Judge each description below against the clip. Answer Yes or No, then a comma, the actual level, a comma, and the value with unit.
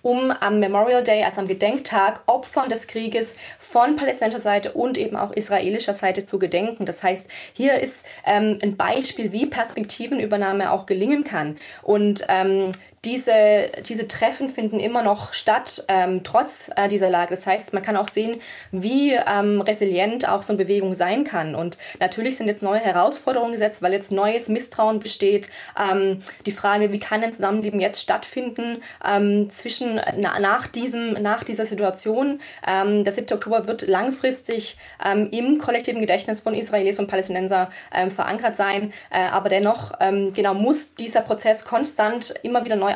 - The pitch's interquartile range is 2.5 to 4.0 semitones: Yes, average, 2.9 semitones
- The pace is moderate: Yes, average, 165 wpm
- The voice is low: No, high, 210 Hz